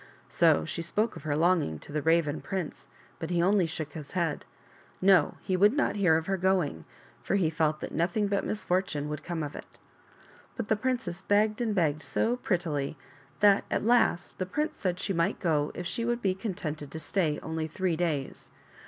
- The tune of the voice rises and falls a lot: No, average, 4.2 semitones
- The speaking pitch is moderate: Yes, medium, 175 Hz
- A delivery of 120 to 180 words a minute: No, average, 195 wpm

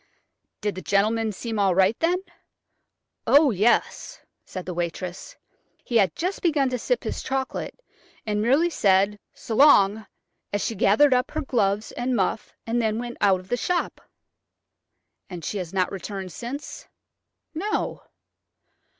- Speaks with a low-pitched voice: No, high, 220 Hz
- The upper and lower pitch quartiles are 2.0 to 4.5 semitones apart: No, wide, 5.4 semitones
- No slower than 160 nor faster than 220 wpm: No, average, 150 wpm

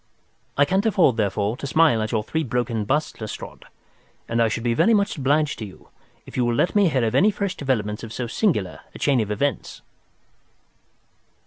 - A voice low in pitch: Yes, low, 125 Hz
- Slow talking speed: No, average, 200 wpm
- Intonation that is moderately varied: No, wide, 6.0 semitones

